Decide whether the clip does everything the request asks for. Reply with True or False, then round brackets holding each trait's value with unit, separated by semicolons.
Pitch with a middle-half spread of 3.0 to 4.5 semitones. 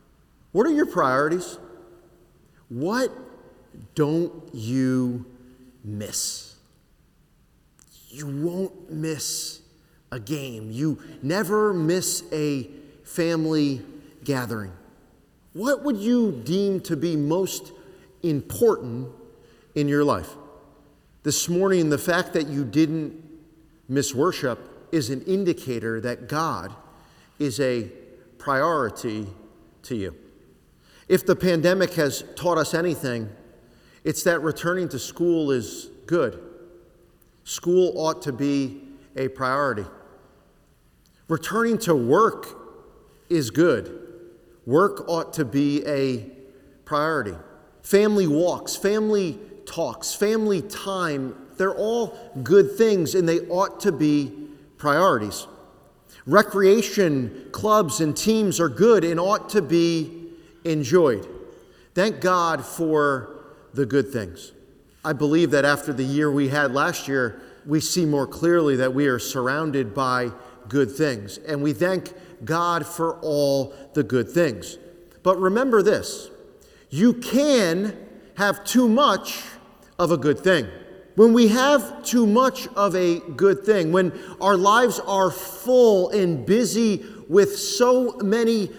False (5.4 semitones)